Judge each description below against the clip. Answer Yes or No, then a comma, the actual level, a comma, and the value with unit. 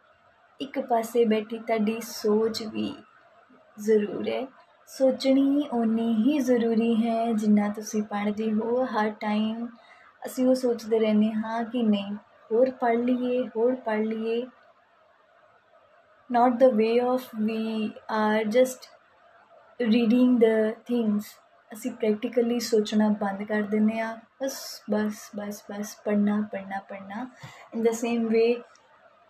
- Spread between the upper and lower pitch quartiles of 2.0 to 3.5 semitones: Yes, narrow, 2.5 semitones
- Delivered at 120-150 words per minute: Yes, average, 125 wpm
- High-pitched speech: Yes, high, 230 Hz